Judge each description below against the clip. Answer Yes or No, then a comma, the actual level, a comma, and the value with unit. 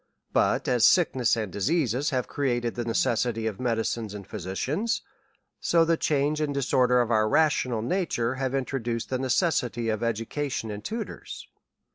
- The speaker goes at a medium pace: Yes, average, 160 wpm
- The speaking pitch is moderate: No, low, 125 Hz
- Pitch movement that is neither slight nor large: Yes, average, 4.0 semitones